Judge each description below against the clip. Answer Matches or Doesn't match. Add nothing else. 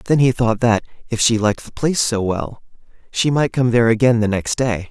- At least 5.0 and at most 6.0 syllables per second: Matches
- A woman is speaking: Doesn't match